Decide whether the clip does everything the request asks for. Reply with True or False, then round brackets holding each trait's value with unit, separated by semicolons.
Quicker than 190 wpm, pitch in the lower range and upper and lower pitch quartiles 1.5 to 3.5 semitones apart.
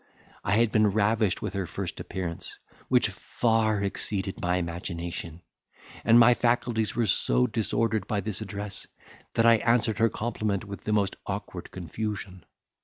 False (150 wpm; 105 Hz; 3.0 semitones)